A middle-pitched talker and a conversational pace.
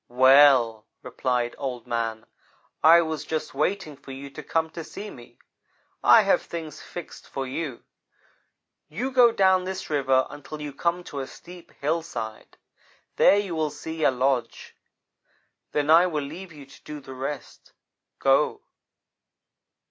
Yes: medium, 150 Hz; average, 150 wpm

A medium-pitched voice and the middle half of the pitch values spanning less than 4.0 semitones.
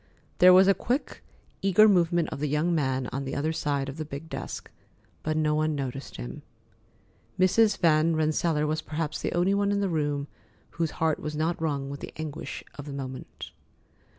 Yes: medium, 155 Hz; average, 3.3 semitones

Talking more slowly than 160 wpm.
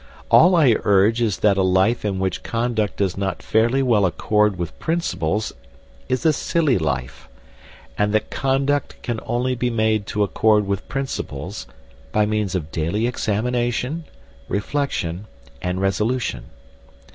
Yes: average, 140 wpm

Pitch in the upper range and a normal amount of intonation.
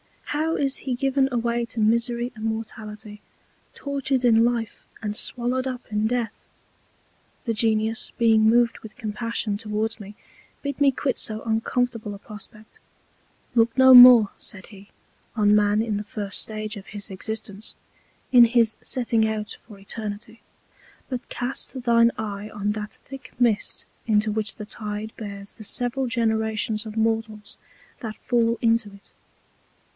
No: high, 225 Hz; narrow, 2.2 semitones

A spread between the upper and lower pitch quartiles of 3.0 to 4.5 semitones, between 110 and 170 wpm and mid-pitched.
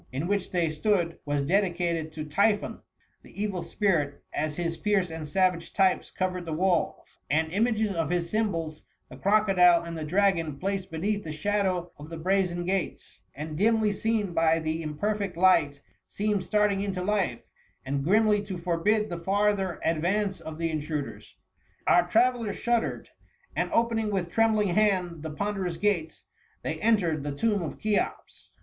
Yes: average, 4.0 semitones; average, 160 wpm; medium, 180 Hz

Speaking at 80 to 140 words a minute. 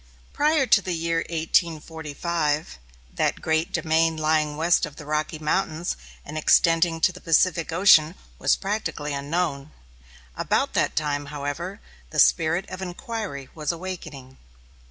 Yes: slow, 135 wpm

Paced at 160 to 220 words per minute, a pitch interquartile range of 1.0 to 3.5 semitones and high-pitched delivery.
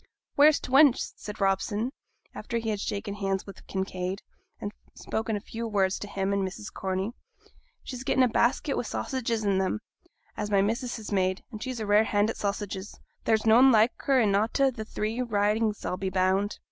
Yes: average, 195 wpm; average, 2.8 semitones; high, 210 Hz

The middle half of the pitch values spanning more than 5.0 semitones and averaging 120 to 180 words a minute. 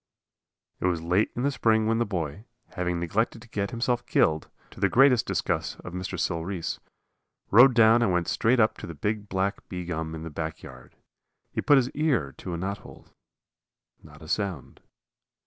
No: wide, 5.4 semitones; average, 190 wpm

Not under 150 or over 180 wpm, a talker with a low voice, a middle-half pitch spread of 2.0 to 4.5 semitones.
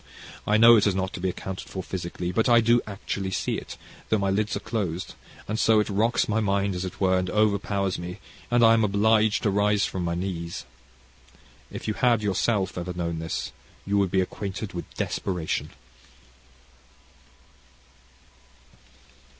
Yes: average, 170 wpm; low, 100 Hz; average, 2.7 semitones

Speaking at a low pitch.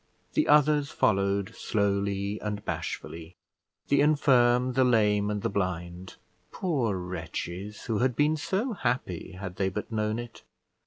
Yes: low, 105 Hz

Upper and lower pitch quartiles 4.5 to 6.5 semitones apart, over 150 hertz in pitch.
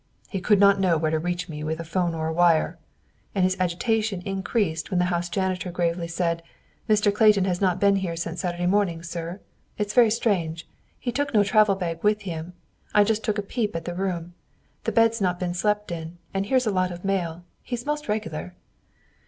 No: average, 3.5 semitones; medium, 185 Hz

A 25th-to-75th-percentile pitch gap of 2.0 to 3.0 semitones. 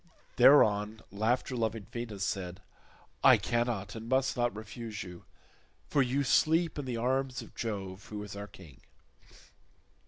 No: average, 3.8 semitones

